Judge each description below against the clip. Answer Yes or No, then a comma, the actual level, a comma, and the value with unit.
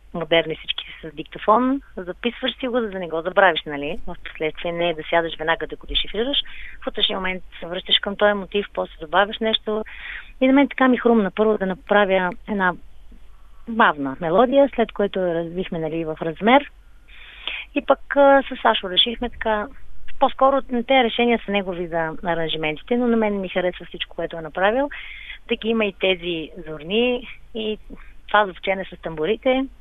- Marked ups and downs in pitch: Yes, wide, 5.7 semitones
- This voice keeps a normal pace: No, fast, 175 wpm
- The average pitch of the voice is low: No, high, 200 Hz